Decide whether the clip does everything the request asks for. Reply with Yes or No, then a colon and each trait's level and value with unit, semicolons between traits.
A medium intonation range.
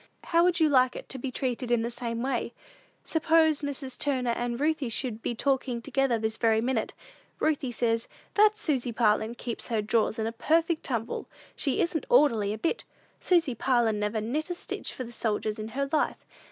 Yes: average, 4.4 semitones